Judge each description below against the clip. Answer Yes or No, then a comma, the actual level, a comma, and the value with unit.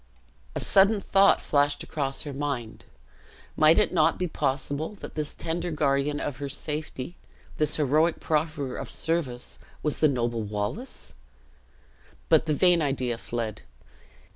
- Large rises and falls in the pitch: No, average, 3.2 semitones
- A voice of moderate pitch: Yes, medium, 150 Hz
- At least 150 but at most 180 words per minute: No, average, 140 wpm